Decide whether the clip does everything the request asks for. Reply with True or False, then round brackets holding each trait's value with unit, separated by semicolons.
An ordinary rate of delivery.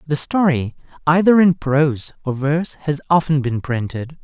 True (155 wpm)